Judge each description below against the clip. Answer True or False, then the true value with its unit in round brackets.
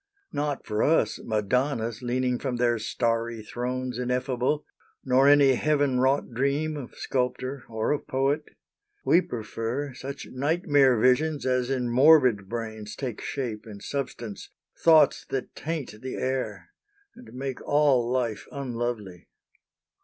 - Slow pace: True (130 wpm)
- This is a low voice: True (130 Hz)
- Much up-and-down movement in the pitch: False (3.0 semitones)